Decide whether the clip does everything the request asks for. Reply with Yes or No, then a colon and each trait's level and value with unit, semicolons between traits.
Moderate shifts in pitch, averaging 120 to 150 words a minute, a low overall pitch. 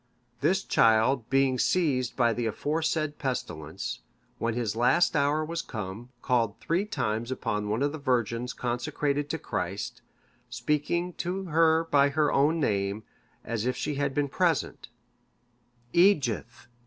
Yes: average, 5.0 semitones; average, 140 wpm; low, 130 Hz